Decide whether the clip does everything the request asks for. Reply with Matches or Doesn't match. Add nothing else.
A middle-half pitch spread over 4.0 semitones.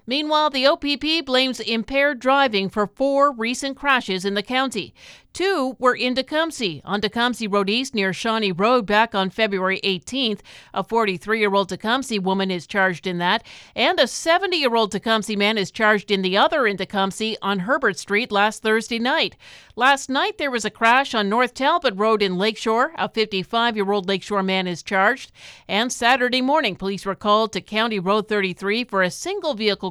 Matches